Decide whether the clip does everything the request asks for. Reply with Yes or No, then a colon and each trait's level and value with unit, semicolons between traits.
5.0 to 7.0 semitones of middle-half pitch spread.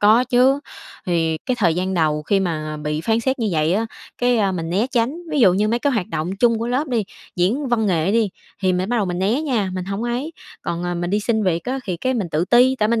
Yes: wide, 5.5 semitones